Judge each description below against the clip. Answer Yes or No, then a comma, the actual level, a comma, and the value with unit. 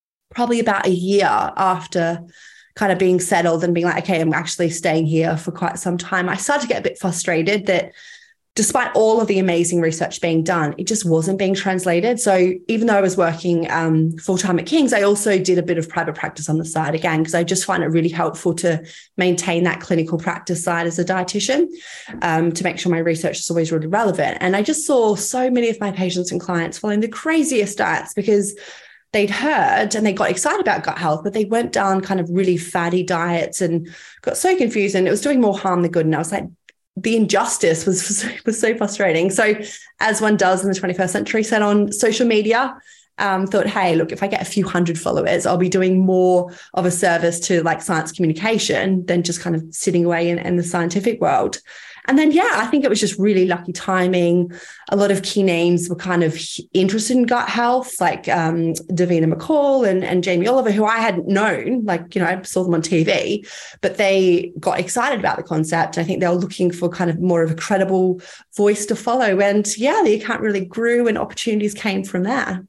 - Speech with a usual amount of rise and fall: Yes, average, 3.6 semitones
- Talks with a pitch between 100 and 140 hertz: No, medium, 185 Hz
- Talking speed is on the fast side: Yes, fast, 220 wpm